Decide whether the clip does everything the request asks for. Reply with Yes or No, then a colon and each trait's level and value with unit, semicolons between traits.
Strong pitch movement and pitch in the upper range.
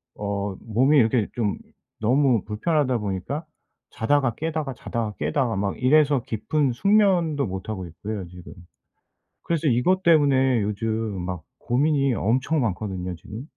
No: wide, 5.9 semitones; low, 120 Hz